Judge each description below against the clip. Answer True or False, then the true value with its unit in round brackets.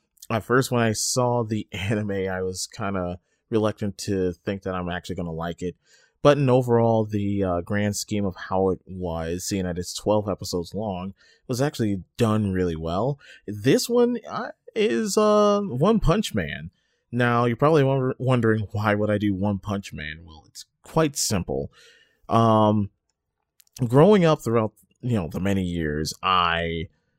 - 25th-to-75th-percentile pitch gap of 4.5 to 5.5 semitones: True (5.0 semitones)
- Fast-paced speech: False (165 wpm)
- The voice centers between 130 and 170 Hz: False (105 Hz)